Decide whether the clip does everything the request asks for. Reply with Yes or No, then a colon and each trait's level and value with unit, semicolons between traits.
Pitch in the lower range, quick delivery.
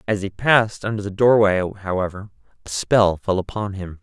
No: low, 100 Hz; average, 180 wpm